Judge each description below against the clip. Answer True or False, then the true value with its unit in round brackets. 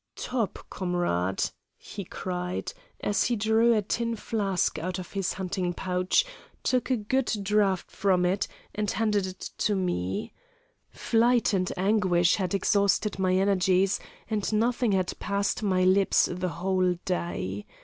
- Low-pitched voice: False (190 Hz)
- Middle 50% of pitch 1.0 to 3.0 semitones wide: True (2.6 semitones)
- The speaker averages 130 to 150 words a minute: True (140 wpm)